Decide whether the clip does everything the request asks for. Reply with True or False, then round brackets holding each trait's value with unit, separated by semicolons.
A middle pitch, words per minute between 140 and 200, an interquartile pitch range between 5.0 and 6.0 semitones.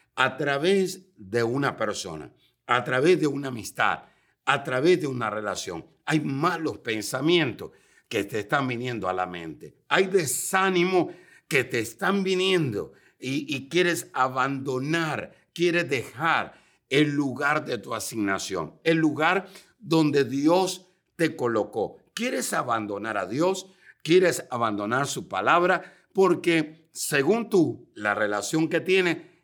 False (155 Hz; 130 wpm; 5.6 semitones)